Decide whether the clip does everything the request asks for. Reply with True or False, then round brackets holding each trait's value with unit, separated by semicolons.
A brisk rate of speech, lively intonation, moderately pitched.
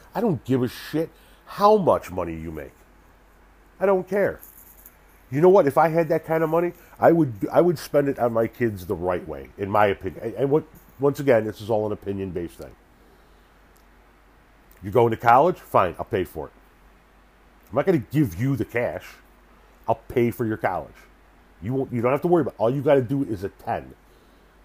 False (210 wpm; 8.8 semitones; 120 Hz)